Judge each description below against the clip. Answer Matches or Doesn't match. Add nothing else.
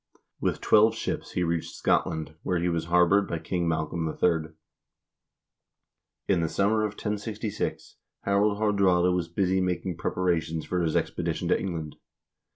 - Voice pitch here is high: Doesn't match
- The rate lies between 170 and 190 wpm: Doesn't match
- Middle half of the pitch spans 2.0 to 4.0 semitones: Matches